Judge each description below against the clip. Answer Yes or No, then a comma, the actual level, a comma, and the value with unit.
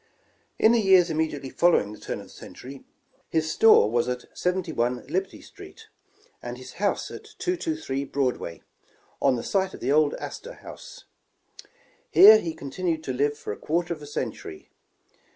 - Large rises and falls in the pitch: Yes, wide, 6.2 semitones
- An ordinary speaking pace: Yes, average, 165 wpm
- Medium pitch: Yes, medium, 155 Hz